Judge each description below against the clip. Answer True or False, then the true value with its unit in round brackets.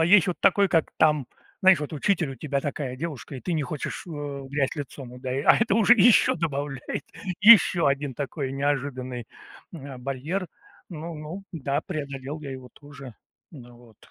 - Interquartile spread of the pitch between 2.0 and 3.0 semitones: False (3.7 semitones)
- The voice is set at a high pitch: False (145 Hz)